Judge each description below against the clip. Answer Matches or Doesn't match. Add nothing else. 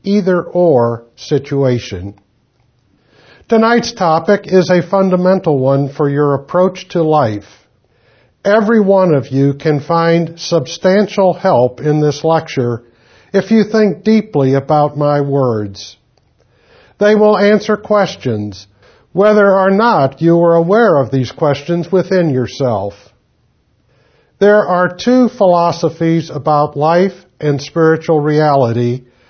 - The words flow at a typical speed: Doesn't match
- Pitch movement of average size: Doesn't match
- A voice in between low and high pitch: Matches